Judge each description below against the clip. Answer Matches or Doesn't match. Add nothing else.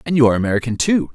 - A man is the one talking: Matches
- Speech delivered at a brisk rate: Matches